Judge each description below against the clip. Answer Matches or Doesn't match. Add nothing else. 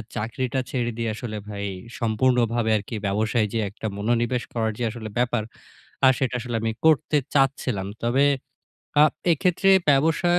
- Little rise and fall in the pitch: Doesn't match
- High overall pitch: Doesn't match